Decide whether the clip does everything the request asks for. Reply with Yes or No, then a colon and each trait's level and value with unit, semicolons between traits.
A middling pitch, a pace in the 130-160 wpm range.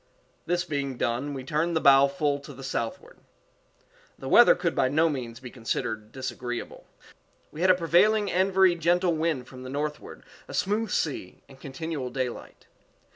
No: medium, 145 Hz; average, 170 wpm